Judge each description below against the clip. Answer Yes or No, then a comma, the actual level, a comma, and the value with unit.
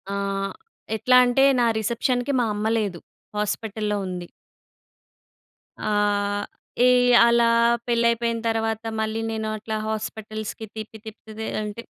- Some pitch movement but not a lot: No, narrow, 1.9 semitones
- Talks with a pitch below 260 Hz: Yes, high, 220 Hz